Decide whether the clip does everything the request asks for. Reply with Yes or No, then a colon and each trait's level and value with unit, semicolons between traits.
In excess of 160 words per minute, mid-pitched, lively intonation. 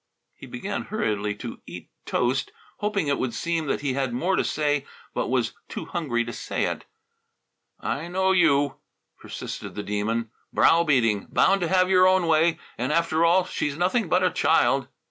Yes: average, 180 wpm; medium, 155 Hz; wide, 6.4 semitones